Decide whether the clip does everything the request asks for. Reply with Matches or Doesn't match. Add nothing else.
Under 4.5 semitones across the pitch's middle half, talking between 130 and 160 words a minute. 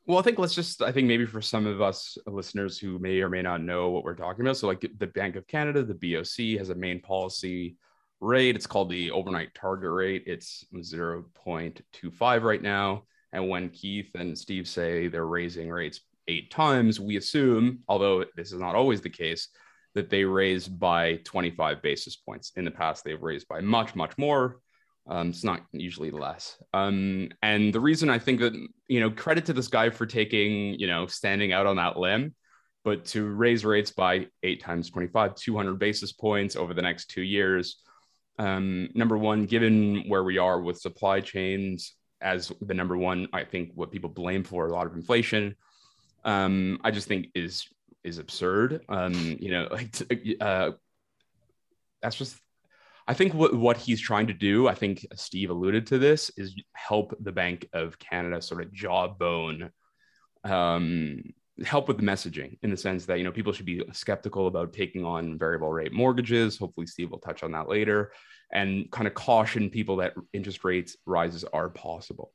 Doesn't match